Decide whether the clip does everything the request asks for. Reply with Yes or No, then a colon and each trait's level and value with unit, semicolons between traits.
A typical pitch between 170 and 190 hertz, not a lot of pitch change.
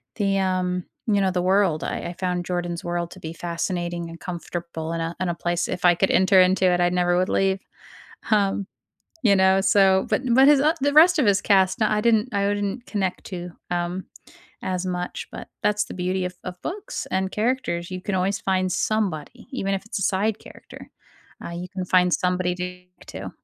Yes: medium, 185 Hz; narrow, 2.2 semitones